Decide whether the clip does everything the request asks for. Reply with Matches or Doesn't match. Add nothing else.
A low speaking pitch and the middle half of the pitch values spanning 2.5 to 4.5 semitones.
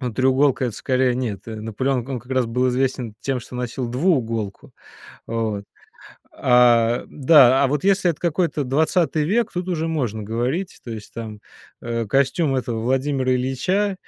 Matches